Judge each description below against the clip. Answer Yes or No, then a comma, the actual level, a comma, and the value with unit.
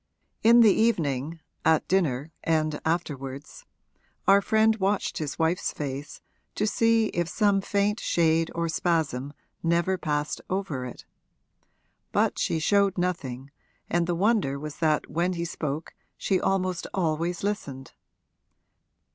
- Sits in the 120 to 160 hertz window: No, medium, 170 Hz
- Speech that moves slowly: Yes, slow, 130 wpm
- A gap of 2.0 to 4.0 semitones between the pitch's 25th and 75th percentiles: No, average, 4.5 semitones